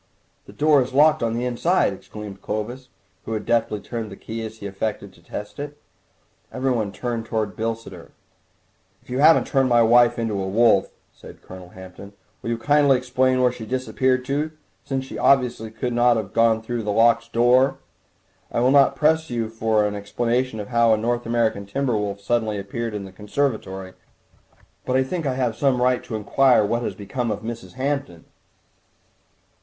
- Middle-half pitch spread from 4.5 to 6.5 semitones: No, average, 3.2 semitones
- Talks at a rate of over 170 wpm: Yes, average, 185 wpm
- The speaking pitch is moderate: No, low, 115 Hz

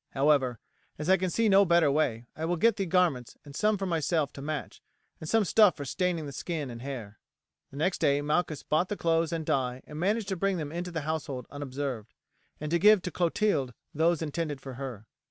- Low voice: No, medium, 160 Hz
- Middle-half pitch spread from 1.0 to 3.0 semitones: No, average, 4.4 semitones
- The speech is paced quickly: Yes, fast, 215 wpm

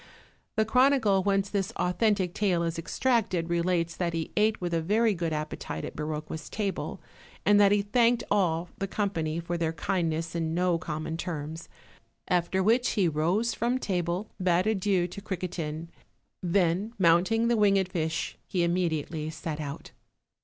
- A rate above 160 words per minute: No, average, 155 wpm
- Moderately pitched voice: Yes, medium, 180 Hz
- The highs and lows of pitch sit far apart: No, average, 3.7 semitones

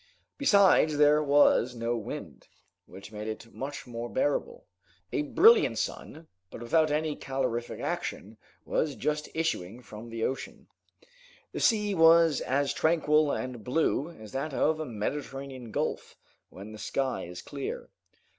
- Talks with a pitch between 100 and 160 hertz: Yes, medium, 140 Hz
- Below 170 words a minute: Yes, average, 140 wpm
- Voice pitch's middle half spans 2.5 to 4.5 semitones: No, average, 5.1 semitones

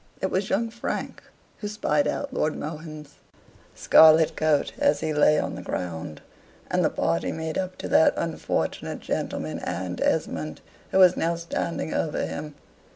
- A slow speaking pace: No, average, 160 wpm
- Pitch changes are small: No, average, 3.8 semitones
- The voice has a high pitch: No, medium, 160 Hz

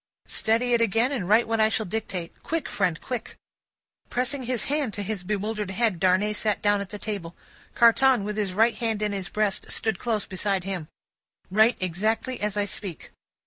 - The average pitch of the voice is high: Yes, high, 210 Hz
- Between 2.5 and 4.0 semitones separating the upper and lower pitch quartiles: Yes, average, 2.8 semitones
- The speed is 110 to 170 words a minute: No, average, 185 wpm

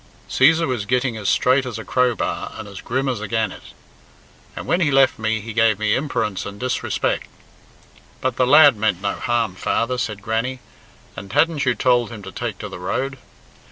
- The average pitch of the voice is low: Yes, low, 115 Hz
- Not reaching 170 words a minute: No, average, 190 wpm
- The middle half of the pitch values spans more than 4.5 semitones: No, average, 3.5 semitones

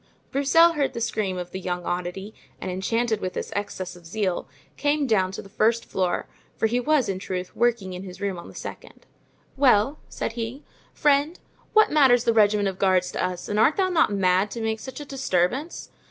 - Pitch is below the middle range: No, high, 215 Hz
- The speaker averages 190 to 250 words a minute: Yes, fast, 205 wpm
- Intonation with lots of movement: Yes, wide, 6.2 semitones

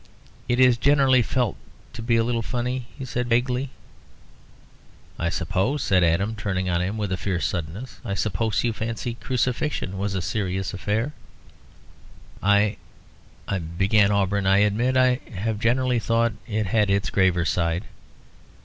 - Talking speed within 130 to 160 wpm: Yes, average, 155 wpm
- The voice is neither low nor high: No, low, 110 Hz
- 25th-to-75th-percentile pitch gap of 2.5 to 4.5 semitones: Yes, average, 4.1 semitones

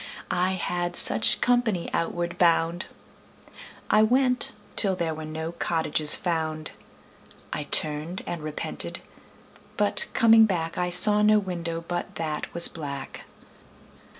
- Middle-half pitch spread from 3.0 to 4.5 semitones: Yes, average, 3.3 semitones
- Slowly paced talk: Yes, slow, 125 wpm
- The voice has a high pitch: No, medium, 175 Hz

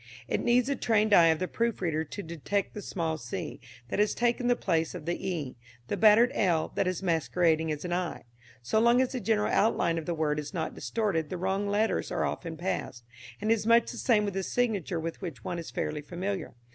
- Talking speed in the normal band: No, fast, 230 wpm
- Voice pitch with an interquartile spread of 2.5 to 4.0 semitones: No, average, 4.7 semitones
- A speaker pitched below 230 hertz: Yes, medium, 185 Hz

